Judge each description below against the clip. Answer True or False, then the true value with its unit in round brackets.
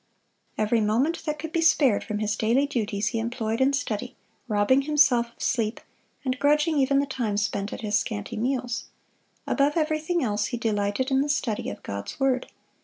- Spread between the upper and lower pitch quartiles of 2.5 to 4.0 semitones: False (4.7 semitones)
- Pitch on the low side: False (245 Hz)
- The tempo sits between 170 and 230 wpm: True (180 wpm)